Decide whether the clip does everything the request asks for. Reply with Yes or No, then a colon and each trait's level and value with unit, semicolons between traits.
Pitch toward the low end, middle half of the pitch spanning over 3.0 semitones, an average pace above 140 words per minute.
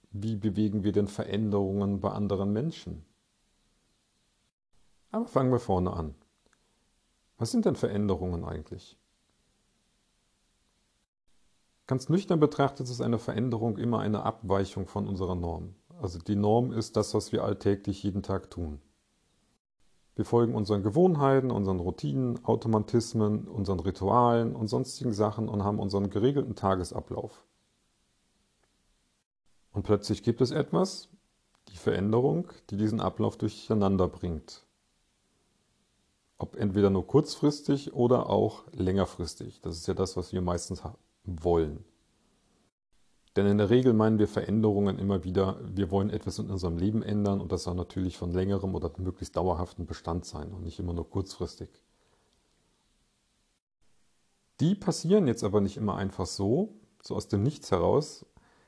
No: low, 100 Hz; average, 3.5 semitones; average, 135 wpm